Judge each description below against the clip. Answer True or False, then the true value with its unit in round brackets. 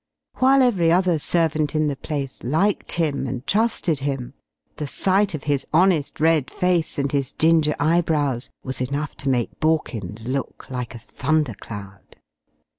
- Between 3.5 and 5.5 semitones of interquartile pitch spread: True (3.9 semitones)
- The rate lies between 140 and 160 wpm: True (150 wpm)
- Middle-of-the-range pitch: True (150 Hz)